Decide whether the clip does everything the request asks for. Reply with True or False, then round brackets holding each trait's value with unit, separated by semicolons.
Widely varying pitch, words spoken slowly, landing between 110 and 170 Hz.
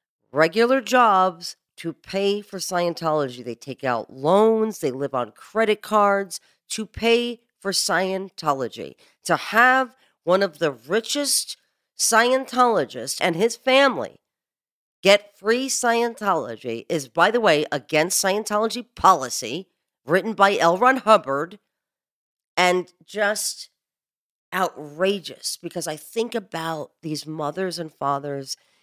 False (6.2 semitones; 115 wpm; 190 Hz)